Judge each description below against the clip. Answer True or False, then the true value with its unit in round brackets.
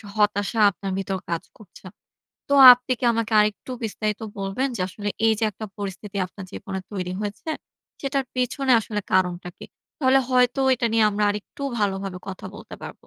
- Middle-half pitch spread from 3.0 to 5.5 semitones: True (3.8 semitones)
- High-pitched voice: True (210 Hz)